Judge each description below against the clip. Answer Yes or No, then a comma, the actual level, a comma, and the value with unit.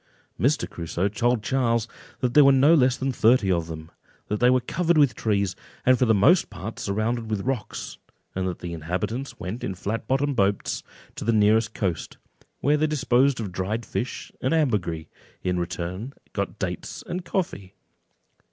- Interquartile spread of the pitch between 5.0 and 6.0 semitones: Yes, average, 5.3 semitones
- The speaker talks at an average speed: Yes, average, 180 wpm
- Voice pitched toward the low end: Yes, low, 115 Hz